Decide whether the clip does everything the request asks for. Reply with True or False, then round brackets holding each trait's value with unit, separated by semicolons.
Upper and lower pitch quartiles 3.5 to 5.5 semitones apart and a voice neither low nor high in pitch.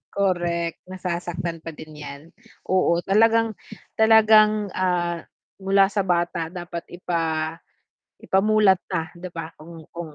False (2.6 semitones; 175 Hz)